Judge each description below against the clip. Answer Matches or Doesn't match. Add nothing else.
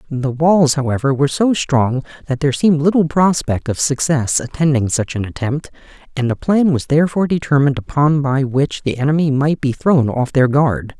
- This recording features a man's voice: Matches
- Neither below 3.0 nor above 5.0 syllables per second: Doesn't match